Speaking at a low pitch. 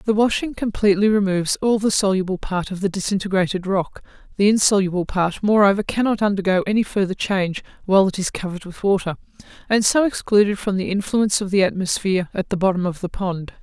No: high, 195 Hz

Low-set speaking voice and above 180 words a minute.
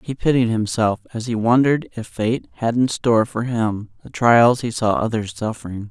Yes: low, 115 Hz; average, 195 wpm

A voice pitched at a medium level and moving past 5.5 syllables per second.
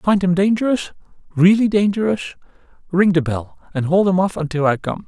Yes: medium, 180 Hz; 6.3 syllables/s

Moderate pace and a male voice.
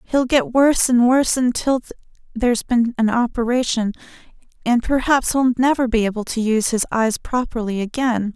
No: average, 165 wpm; female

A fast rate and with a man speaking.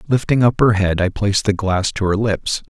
Yes: fast, 240 wpm; male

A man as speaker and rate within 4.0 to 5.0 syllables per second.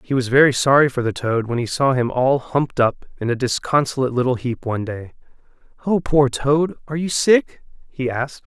No: male; 5.6 syllables/s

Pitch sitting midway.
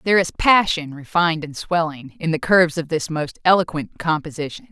Yes: medium, 165 Hz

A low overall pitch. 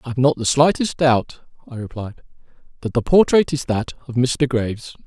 Yes: low, 130 Hz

